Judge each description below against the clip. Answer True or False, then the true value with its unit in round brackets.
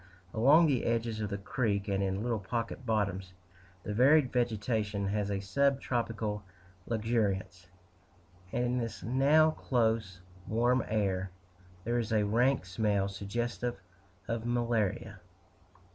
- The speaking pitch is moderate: False (110 Hz)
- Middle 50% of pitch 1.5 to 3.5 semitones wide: True (3.2 semitones)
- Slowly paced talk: True (130 wpm)